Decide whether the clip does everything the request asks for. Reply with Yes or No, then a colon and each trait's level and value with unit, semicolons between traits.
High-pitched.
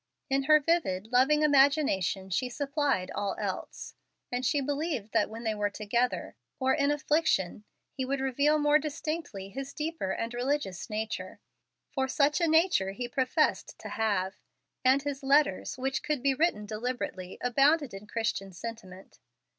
Yes: very high, 260 Hz